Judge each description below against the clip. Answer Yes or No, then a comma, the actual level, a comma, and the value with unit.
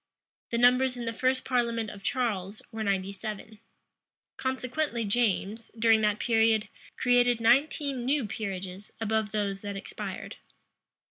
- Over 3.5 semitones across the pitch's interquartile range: No, average, 3.0 semitones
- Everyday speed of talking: No, slow, 130 wpm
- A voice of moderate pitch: No, high, 225 Hz